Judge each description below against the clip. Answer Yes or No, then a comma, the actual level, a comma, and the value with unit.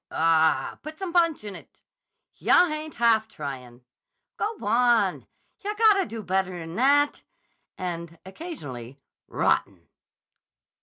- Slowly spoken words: Yes, slow, 115 wpm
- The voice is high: Yes, high, 215 Hz